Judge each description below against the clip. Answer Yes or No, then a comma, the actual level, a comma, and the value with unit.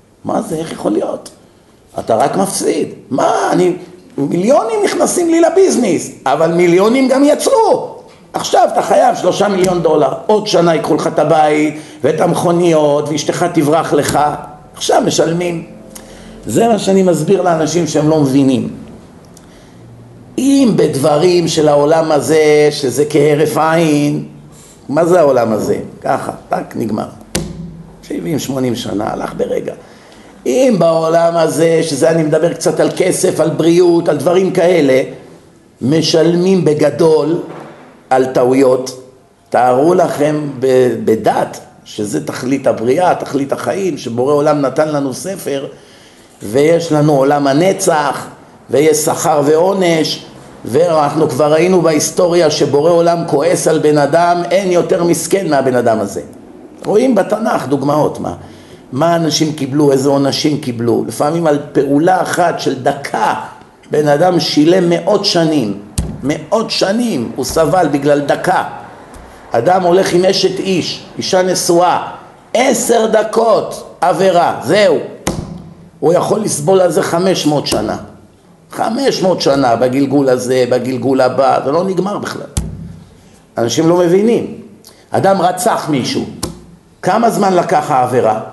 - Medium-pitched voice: Yes, medium, 160 Hz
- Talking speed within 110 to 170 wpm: Yes, average, 125 wpm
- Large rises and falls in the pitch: No, average, 3.8 semitones